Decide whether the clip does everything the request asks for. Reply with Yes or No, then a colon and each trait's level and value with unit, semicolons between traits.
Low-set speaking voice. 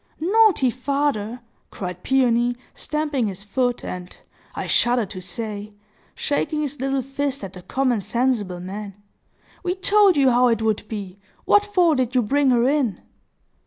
No: high, 245 Hz